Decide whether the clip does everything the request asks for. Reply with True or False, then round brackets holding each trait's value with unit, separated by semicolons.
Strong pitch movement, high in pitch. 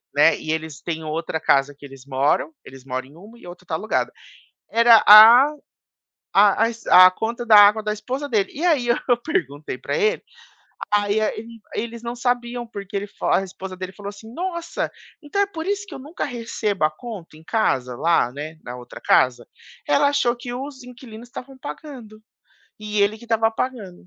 True (6.3 semitones; 215 Hz)